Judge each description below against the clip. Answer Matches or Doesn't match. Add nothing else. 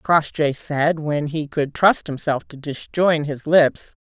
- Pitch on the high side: Doesn't match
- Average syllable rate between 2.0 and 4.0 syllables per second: Matches